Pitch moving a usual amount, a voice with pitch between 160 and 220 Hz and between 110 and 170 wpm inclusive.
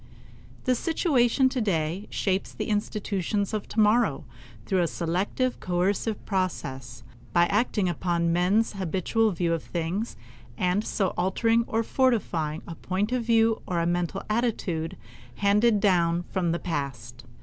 Yes: average, 4.5 semitones; high, 190 Hz; average, 140 wpm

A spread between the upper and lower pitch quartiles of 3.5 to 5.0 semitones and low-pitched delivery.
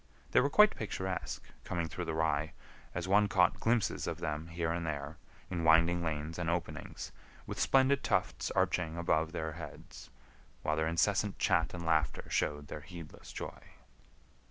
No: narrow, 2.4 semitones; very low, 85 Hz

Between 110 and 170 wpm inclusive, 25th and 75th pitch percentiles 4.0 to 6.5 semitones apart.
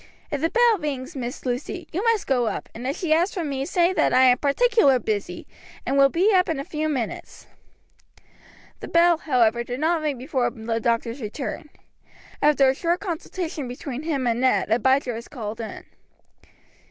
No: average, 190 wpm; average, 5.1 semitones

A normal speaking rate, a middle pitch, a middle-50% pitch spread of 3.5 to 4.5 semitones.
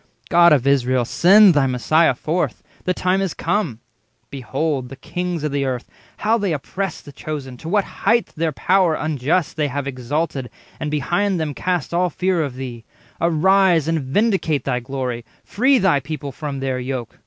No: average, 175 wpm; medium, 155 Hz; average, 5.1 semitones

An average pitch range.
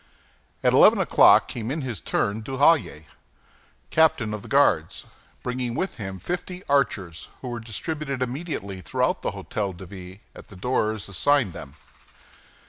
No: wide, 6.4 semitones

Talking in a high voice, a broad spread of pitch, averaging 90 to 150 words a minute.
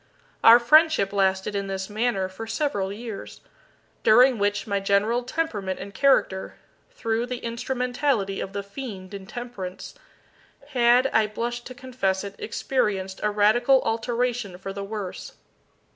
No: high, 220 Hz; average, 3.8 semitones; slow, 135 wpm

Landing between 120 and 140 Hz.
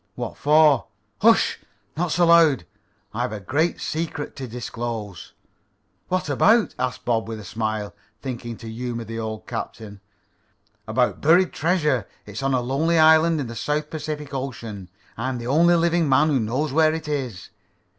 Yes: low, 135 Hz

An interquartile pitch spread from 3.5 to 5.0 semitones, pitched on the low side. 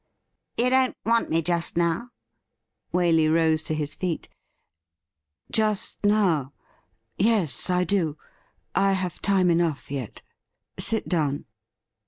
No: average, 4.3 semitones; medium, 170 Hz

